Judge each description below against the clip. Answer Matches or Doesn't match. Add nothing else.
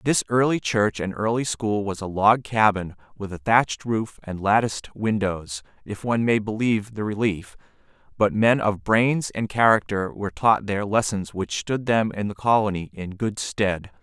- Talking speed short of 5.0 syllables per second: Matches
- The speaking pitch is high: Doesn't match